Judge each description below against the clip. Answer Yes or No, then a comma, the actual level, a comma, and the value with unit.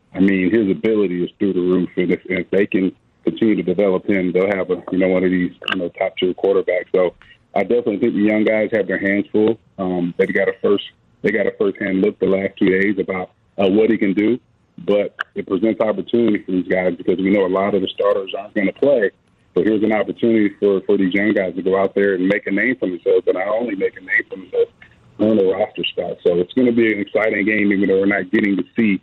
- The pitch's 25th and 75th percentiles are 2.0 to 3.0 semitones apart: Yes, average, 2.7 semitones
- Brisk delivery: Yes, fast, 260 wpm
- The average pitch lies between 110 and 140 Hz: No, low, 100 Hz